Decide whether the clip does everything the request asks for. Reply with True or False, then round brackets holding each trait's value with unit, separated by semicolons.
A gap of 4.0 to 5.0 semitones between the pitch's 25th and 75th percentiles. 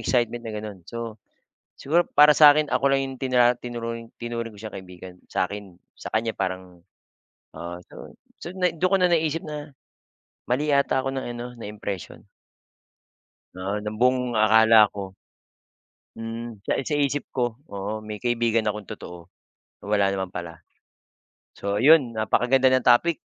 True (4.4 semitones)